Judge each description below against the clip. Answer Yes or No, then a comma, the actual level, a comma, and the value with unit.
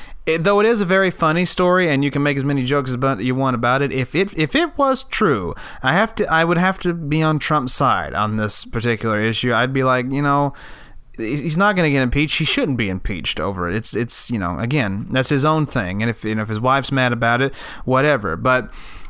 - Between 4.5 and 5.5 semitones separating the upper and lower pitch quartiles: Yes, average, 5.1 semitones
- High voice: No, low, 135 Hz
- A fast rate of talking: Yes, fast, 250 wpm